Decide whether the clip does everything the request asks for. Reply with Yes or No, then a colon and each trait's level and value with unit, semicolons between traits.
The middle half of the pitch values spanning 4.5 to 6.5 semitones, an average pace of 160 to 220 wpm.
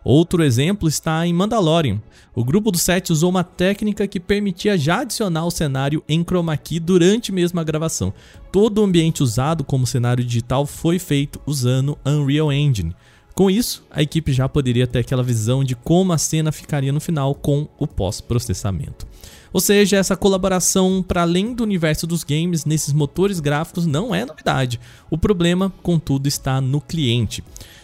Yes: average, 5.0 semitones; average, 170 wpm